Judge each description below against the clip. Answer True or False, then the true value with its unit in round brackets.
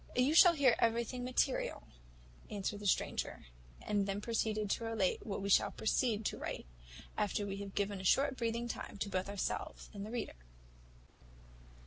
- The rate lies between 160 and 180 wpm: True (165 wpm)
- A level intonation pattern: False (3.0 semitones)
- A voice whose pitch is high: True (215 Hz)